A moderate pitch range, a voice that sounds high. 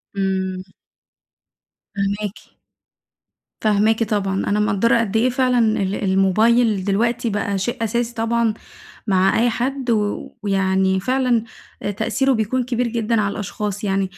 Yes: average, 3.1 semitones; high, 215 Hz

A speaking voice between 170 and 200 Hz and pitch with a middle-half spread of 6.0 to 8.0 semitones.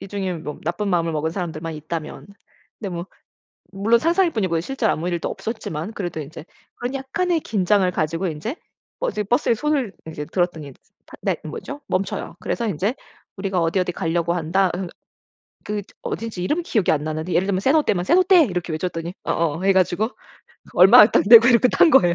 No: high, 190 Hz; wide, 5.4 semitones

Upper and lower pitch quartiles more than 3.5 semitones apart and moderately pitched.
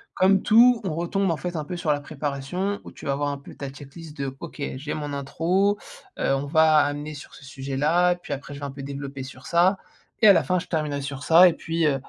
Yes: average, 3.9 semitones; medium, 150 Hz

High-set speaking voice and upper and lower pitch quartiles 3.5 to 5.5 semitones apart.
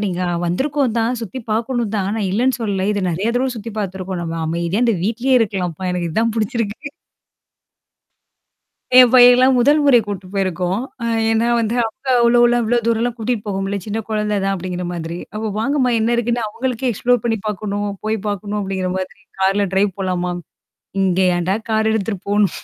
Yes: high, 215 Hz; average, 3.8 semitones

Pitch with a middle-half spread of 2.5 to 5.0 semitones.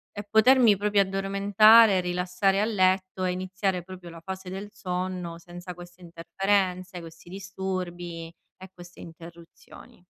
No: narrow, 1.8 semitones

